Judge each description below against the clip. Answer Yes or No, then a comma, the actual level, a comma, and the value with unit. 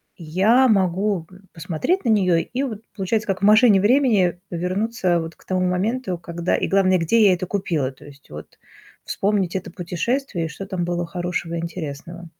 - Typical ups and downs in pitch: Yes, average, 3.5 semitones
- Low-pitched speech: No, medium, 185 Hz